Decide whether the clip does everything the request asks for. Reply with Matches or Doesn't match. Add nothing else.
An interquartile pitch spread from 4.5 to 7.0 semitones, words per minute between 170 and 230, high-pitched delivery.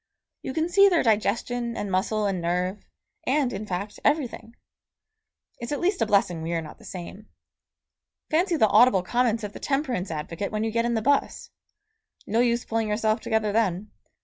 Doesn't match